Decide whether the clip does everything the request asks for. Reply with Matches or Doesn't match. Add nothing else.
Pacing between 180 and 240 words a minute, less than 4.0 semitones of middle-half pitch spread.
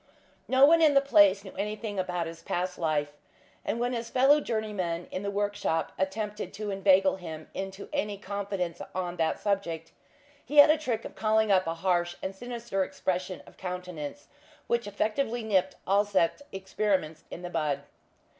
Doesn't match